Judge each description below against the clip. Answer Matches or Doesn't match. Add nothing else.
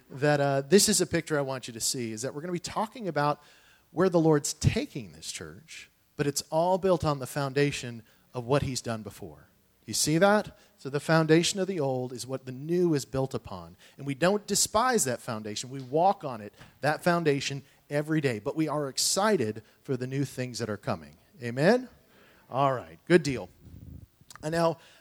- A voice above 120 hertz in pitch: Matches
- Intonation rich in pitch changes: Doesn't match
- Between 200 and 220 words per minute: Matches